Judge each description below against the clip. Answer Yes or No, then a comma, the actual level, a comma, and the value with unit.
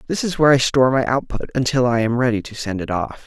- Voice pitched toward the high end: No, low, 125 Hz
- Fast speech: Yes, fast, 275 wpm